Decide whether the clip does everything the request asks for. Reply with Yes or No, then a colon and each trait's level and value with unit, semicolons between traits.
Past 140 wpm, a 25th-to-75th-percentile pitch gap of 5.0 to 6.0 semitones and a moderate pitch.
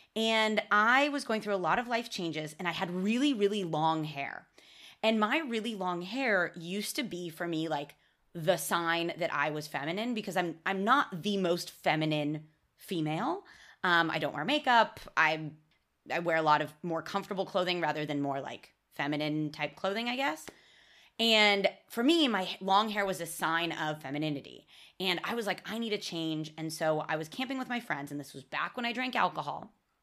Yes: average, 200 wpm; wide, 5.5 semitones; medium, 180 Hz